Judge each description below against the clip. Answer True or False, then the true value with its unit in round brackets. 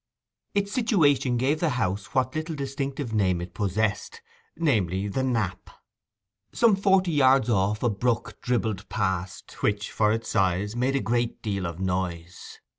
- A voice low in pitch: True (115 Hz)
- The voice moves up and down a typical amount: False (6.1 semitones)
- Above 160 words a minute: False (150 wpm)